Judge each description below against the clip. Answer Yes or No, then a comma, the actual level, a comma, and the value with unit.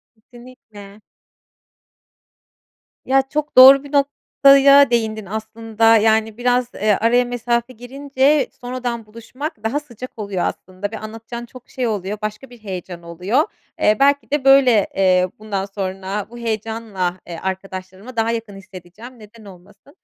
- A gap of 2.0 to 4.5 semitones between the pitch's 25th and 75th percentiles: Yes, average, 3.9 semitones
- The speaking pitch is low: No, high, 225 Hz